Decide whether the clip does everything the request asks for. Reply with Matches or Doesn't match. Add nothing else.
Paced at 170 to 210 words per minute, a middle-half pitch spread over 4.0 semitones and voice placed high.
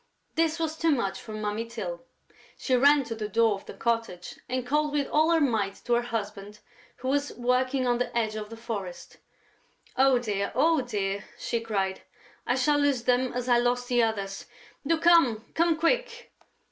Matches